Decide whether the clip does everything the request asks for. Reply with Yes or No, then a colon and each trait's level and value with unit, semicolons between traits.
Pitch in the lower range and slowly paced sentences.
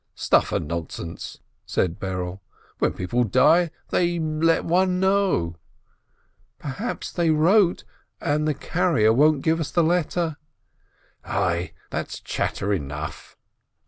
No: medium, 155 Hz; slow, 125 wpm